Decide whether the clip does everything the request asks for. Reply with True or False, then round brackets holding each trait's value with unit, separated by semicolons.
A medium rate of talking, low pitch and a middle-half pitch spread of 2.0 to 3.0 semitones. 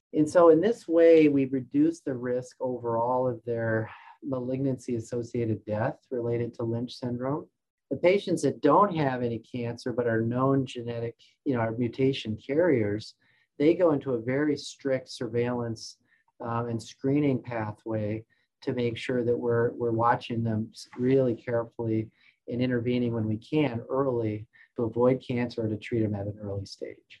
True (160 wpm; 120 Hz; 2.5 semitones)